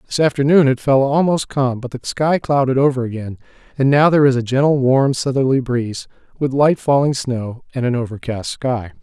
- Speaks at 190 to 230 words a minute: Yes, average, 195 wpm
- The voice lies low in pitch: Yes, low, 130 Hz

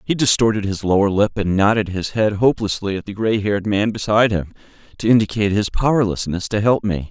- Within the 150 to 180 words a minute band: No, fast, 205 wpm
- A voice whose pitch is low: Yes, low, 105 Hz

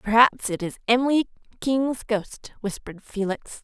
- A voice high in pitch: Yes, high, 225 Hz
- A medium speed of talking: No, slow, 130 wpm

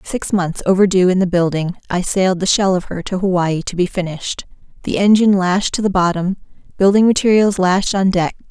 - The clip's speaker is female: Yes, female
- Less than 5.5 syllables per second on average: No, 5.6 syllables/s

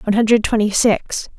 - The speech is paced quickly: No, average, 175 wpm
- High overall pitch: Yes, high, 220 Hz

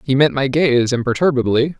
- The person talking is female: No, male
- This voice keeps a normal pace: Yes, average, 165 wpm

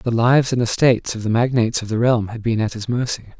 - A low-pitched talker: Yes, low, 115 Hz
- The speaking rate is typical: No, fast, 265 wpm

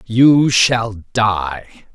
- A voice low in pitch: Yes, low, 110 Hz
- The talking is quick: No, slow, 95 wpm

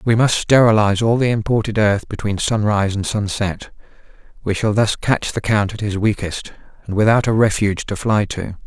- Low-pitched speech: Yes, low, 105 Hz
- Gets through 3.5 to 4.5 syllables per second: No, 5.4 syllables/s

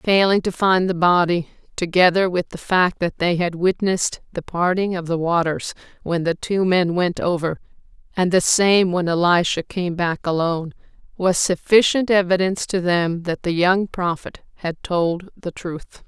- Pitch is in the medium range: Yes, medium, 180 Hz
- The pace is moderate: Yes, average, 170 wpm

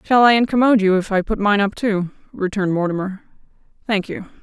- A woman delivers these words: Yes, female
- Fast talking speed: No, average, 190 wpm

